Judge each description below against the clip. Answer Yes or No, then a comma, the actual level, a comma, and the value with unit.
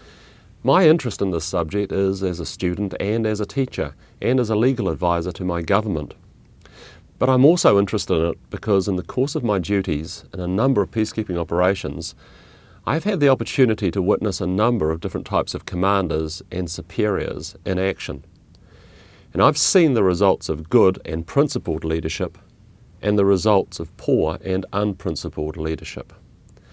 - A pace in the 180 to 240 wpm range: No, average, 170 wpm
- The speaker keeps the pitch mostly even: No, average, 3.8 semitones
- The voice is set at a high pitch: No, very low, 95 Hz